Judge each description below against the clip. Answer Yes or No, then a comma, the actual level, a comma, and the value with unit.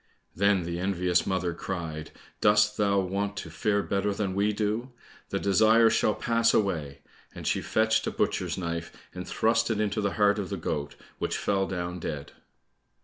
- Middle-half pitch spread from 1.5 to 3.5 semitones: Yes, average, 3.0 semitones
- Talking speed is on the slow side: No, average, 175 wpm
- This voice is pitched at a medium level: No, low, 100 Hz